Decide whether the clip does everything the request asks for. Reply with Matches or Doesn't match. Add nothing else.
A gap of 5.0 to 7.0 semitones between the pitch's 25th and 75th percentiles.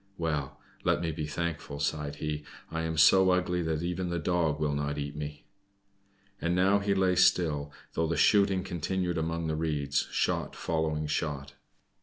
Doesn't match